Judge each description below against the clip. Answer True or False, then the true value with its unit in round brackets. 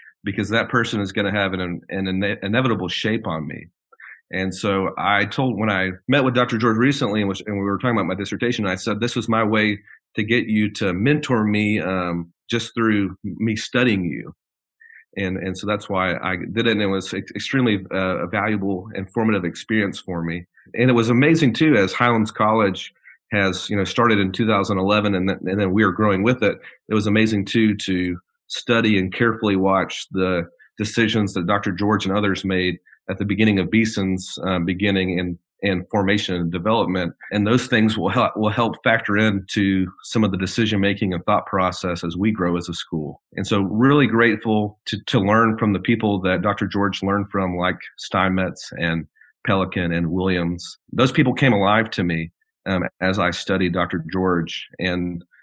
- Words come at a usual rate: True (195 wpm)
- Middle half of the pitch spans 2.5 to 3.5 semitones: True (2.9 semitones)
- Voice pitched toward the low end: True (100 Hz)